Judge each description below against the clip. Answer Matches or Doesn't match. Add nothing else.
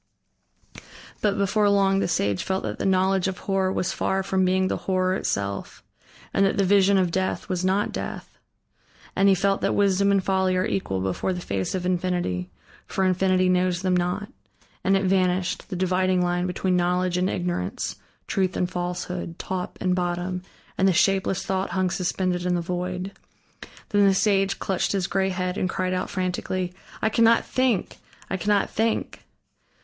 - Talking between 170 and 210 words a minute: Matches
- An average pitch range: Doesn't match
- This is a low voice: Doesn't match